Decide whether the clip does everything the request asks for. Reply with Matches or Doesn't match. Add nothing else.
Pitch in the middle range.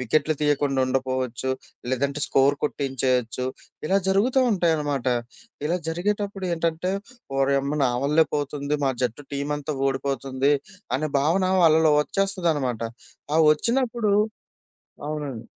Matches